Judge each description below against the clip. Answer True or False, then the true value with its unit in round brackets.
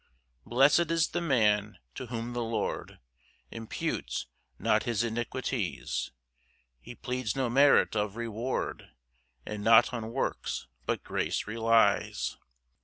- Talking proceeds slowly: True (120 wpm)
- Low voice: True (115 Hz)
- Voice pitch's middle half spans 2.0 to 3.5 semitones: True (2.6 semitones)